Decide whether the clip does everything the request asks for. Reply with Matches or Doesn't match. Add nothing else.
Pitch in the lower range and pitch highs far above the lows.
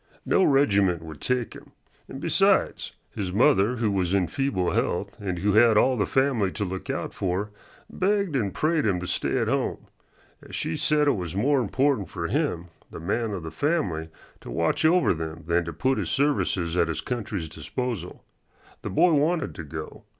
Matches